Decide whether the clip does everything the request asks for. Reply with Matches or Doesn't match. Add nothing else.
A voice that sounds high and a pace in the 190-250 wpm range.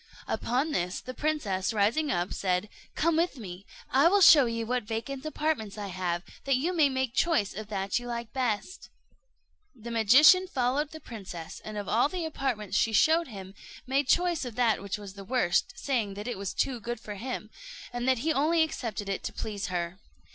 Matches